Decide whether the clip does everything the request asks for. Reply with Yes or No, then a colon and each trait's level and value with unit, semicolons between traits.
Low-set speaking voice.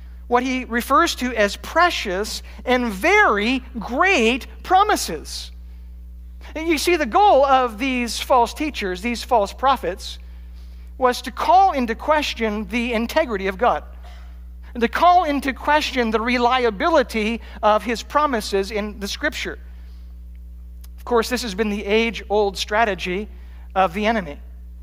No: high, 225 Hz